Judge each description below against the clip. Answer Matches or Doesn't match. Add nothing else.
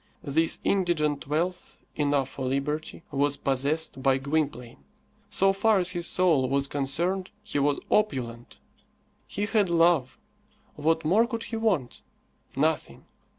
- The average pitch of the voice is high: Doesn't match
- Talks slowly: Matches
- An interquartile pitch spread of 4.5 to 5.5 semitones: Matches